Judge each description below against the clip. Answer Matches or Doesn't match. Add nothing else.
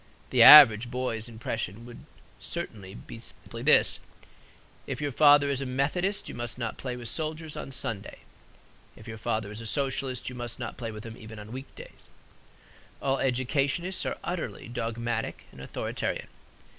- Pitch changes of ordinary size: Matches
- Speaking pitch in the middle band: Doesn't match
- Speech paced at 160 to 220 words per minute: Matches